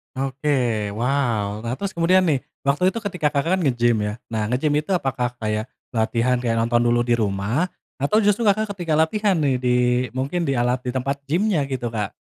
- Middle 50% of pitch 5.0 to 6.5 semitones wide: Yes, wide, 5.5 semitones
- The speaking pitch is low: Yes, low, 130 Hz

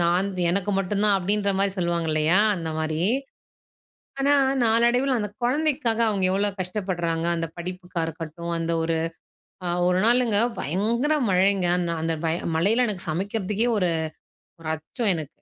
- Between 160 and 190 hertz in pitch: Yes, medium, 185 Hz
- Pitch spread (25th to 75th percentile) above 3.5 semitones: Yes, average, 4.2 semitones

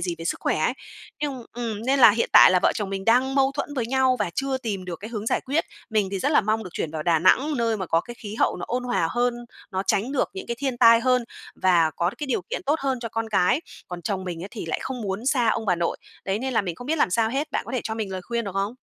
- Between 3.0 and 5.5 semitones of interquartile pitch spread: Yes, average, 5.1 semitones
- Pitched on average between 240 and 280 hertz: No, high, 225 Hz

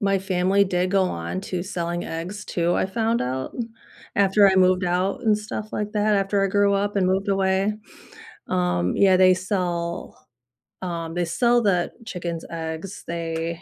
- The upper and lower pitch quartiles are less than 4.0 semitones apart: Yes, average, 2.7 semitones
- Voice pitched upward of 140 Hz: Yes, medium, 185 Hz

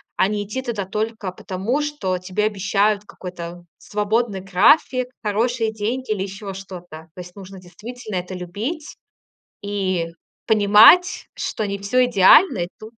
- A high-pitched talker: Yes, high, 205 Hz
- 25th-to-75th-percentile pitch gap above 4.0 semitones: No, average, 3.3 semitones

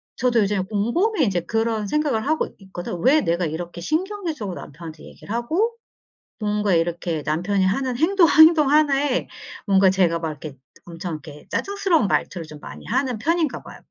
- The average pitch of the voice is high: Yes, high, 210 Hz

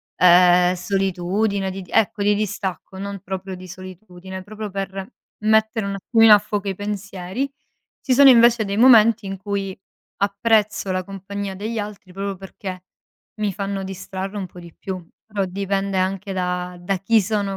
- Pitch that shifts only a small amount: Yes, narrow, 1.9 semitones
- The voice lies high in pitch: Yes, high, 195 Hz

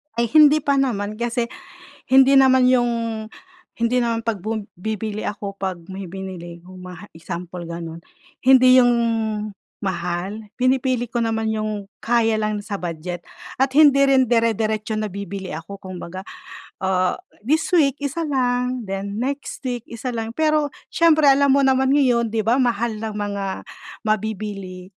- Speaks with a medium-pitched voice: No, high, 225 Hz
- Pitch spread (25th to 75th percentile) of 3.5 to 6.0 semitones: Yes, average, 4.7 semitones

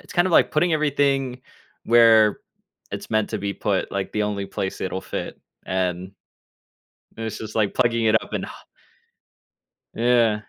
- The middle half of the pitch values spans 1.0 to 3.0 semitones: No, average, 3.6 semitones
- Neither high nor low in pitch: No, low, 110 Hz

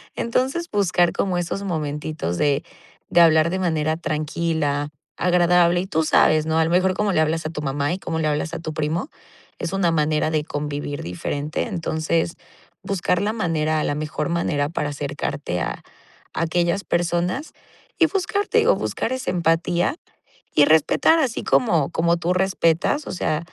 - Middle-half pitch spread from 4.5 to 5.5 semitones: No, average, 2.9 semitones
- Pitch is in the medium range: Yes, medium, 165 Hz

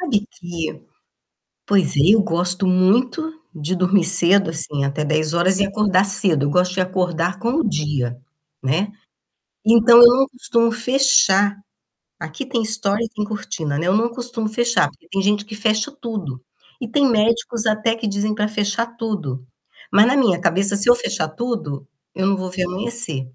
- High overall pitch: Yes, high, 200 Hz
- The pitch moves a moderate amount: Yes, average, 4.7 semitones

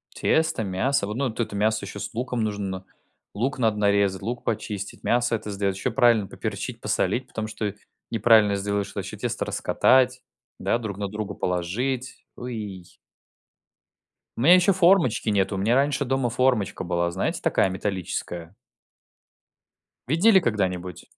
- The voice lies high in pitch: No, low, 110 Hz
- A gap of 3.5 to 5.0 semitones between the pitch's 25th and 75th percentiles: Yes, average, 4.1 semitones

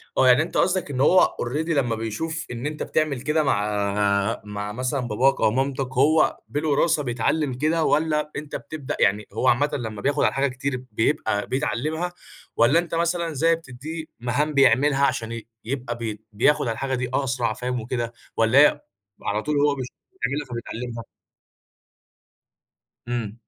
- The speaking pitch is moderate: No, low, 130 Hz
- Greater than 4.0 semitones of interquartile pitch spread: Yes, average, 4.4 semitones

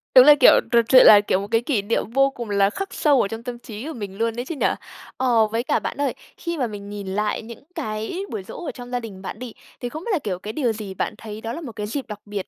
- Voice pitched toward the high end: Yes, high, 230 Hz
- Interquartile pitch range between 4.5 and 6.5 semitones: No, average, 3.9 semitones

